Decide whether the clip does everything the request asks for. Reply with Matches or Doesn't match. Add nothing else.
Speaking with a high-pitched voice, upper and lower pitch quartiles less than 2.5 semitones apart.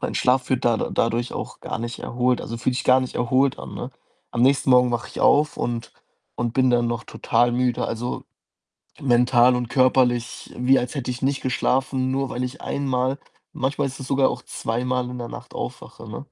Doesn't match